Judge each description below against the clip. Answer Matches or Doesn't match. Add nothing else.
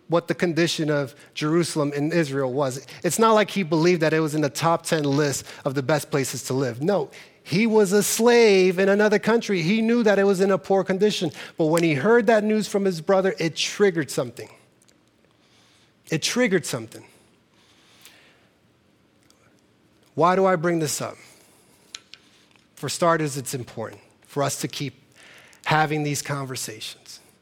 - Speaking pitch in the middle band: Matches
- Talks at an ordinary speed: Matches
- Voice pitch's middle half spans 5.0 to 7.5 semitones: Matches